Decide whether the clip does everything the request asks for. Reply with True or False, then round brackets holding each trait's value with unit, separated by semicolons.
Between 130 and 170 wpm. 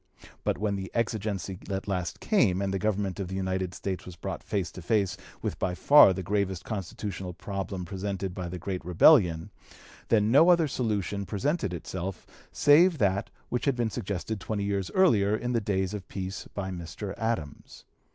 False (180 wpm)